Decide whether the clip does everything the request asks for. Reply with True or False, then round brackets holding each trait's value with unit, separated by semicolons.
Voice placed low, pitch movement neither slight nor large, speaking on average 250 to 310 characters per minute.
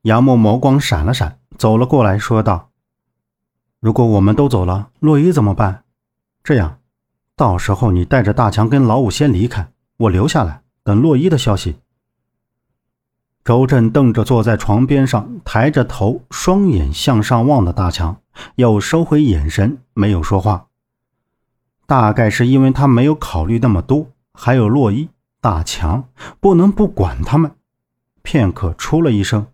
False (115 Hz; 4.8 semitones; 225 characters per minute)